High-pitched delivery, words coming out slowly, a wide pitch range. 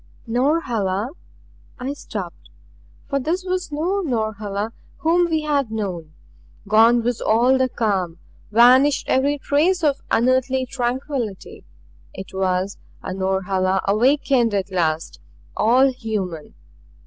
Yes: high, 235 Hz; slow, 115 wpm; wide, 6.0 semitones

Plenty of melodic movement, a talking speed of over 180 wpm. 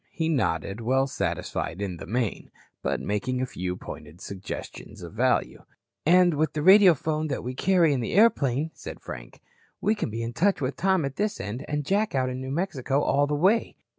Yes: wide, 6.4 semitones; average, 195 wpm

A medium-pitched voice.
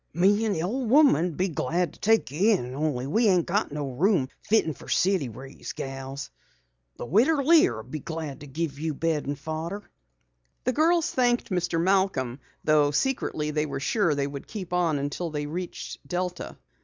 Yes: medium, 165 Hz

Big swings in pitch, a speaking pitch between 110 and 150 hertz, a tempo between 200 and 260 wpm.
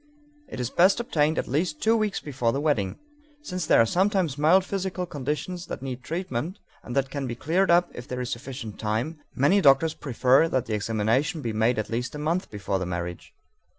Yes: wide, 6.6 semitones; medium, 140 Hz; fast, 205 wpm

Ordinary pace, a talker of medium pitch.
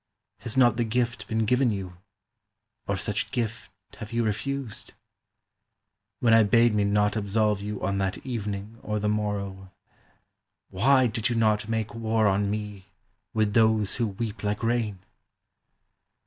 No: average, 150 wpm; low, 110 Hz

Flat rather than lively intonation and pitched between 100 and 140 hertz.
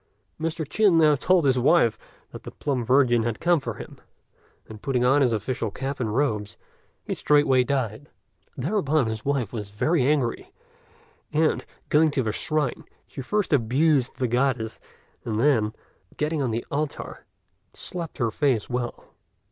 No: average, 4.4 semitones; low, 135 Hz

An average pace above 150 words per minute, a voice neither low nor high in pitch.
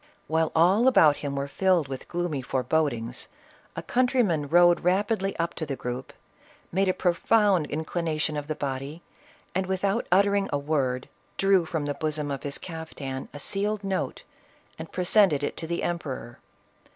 Yes: average, 165 wpm; medium, 160 Hz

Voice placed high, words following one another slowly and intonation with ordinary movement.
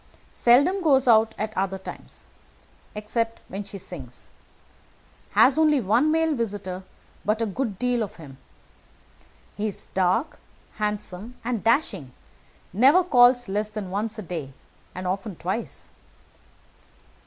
Yes: high, 215 Hz; slow, 130 wpm; average, 4.5 semitones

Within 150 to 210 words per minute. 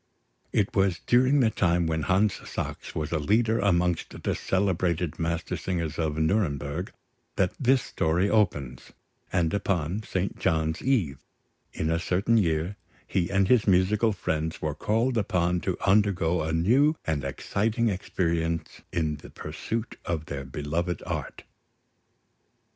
No: slow, 135 wpm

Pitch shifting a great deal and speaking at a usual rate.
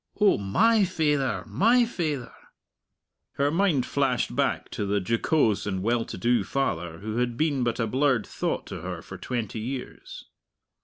Yes: wide, 6.0 semitones; average, 160 wpm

